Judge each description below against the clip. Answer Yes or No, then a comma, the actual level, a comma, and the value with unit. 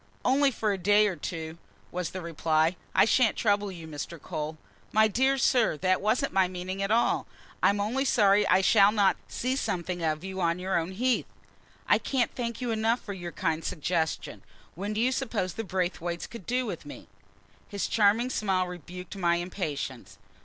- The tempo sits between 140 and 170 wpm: No, average, 185 wpm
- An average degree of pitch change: Yes, average, 4.3 semitones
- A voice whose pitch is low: No, high, 195 Hz